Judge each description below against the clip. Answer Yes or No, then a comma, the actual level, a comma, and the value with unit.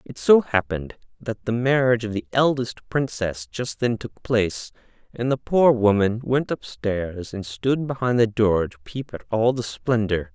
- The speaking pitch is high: No, low, 115 Hz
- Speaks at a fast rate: No, average, 180 wpm